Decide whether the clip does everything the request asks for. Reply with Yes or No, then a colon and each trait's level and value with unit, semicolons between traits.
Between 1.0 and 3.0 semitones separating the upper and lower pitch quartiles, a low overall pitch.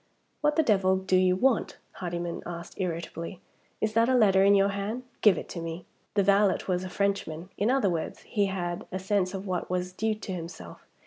No: narrow, 2.4 semitones; high, 190 Hz